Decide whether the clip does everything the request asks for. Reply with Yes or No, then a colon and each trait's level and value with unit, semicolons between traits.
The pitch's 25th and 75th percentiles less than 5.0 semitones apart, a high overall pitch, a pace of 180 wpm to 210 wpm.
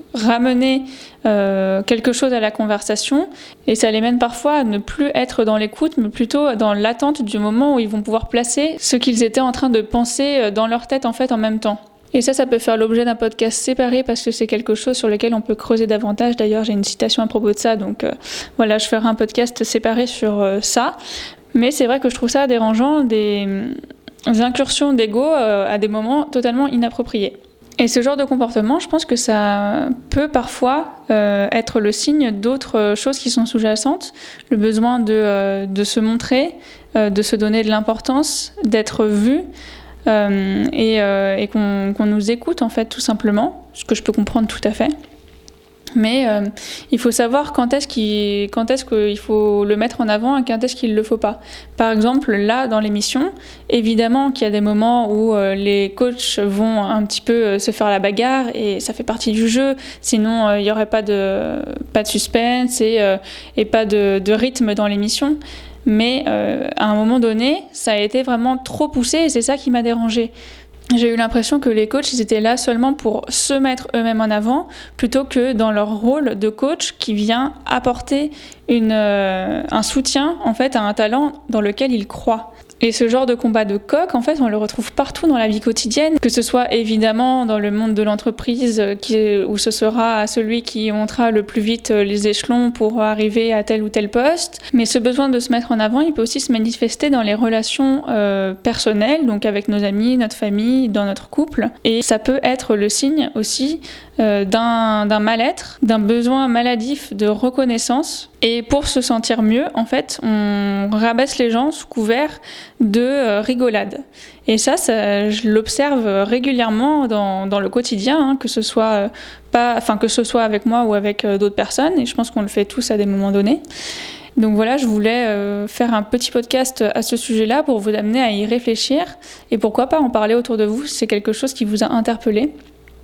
Yes: average, 3.2 semitones; high, 230 Hz; average, 205 wpm